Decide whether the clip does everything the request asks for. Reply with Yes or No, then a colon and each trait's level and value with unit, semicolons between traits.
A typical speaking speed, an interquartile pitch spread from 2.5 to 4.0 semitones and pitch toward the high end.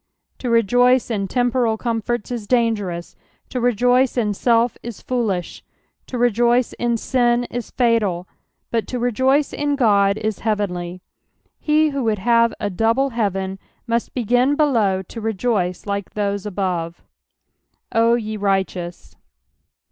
No: slow, 130 wpm; average, 3.4 semitones; high, 230 Hz